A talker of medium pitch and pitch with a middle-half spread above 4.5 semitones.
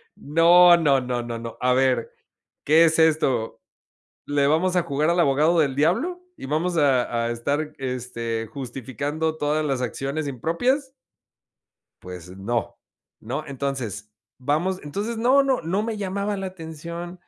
Yes: medium, 150 Hz; wide, 5.4 semitones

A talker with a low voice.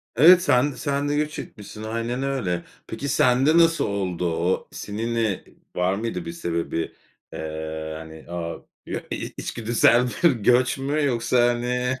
Yes: low, 120 Hz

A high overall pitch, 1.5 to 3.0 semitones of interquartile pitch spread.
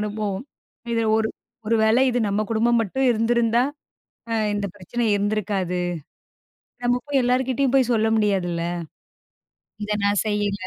Yes: high, 220 Hz; average, 2.7 semitones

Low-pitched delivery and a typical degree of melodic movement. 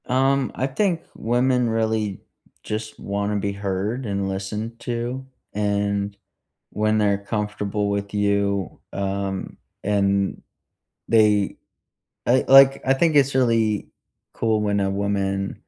Yes: low, 105 Hz; average, 3.0 semitones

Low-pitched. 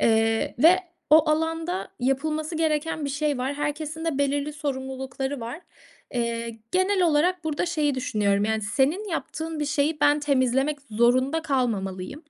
No: very high, 290 Hz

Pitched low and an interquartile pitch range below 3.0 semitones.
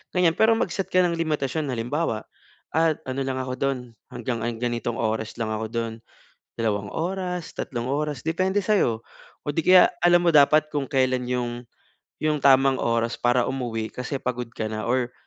No: low, 130 Hz; average, 5.3 semitones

